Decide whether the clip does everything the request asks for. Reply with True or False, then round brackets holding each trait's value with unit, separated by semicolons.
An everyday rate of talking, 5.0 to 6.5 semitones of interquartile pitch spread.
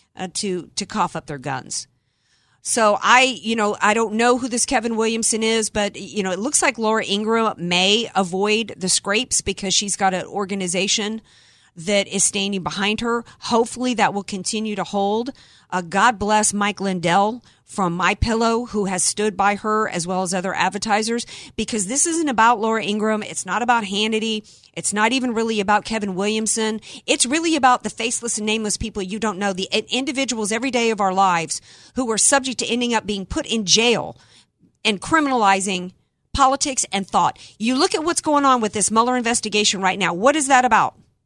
False (190 wpm; 3.0 semitones)